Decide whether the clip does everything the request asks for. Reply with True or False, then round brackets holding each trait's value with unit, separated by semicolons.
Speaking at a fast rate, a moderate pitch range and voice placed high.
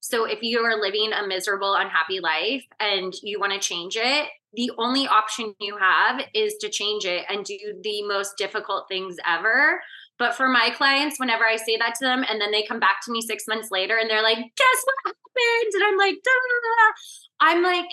False (210 wpm; 6.6 semitones; 225 Hz)